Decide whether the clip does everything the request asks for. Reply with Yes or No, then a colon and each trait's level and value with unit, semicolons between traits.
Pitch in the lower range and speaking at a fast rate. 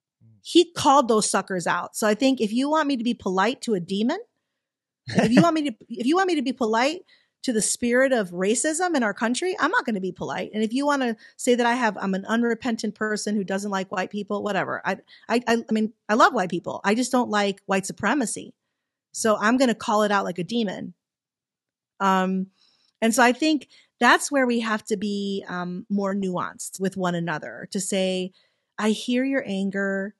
No: high, 215 Hz; fast, 220 wpm